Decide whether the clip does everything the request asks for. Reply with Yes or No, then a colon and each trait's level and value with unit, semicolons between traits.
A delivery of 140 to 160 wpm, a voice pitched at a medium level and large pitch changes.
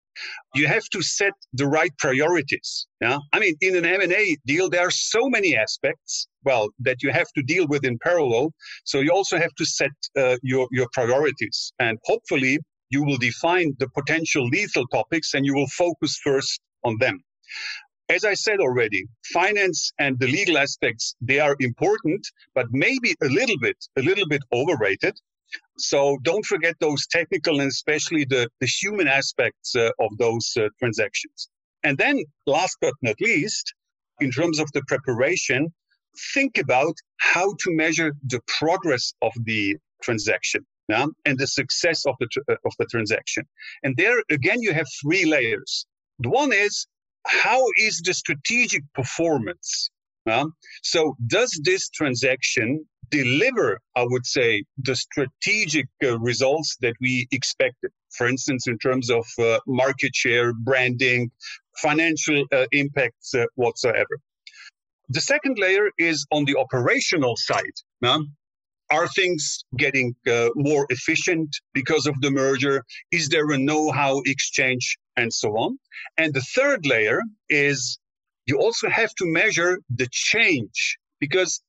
Yes: average, 155 wpm; medium, 150 Hz; wide, 5.7 semitones